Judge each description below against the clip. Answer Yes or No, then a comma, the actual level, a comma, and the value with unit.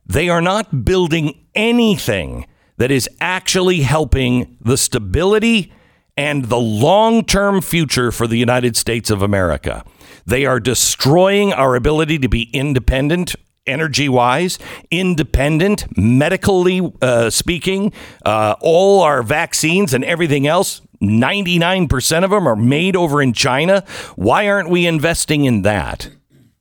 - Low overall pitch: No, medium, 150 Hz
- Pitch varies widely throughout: Yes, wide, 6.7 semitones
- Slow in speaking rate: Yes, slow, 130 wpm